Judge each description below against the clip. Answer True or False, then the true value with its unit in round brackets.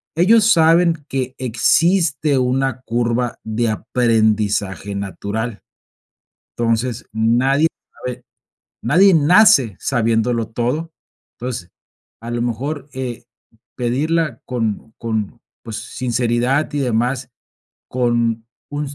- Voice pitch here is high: False (125 Hz)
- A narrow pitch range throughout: False (3.7 semitones)